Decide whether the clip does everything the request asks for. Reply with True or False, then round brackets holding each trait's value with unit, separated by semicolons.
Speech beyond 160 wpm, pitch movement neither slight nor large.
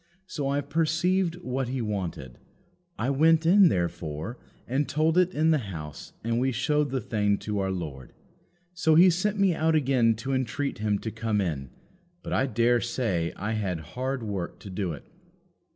False (180 wpm; 7.3 semitones)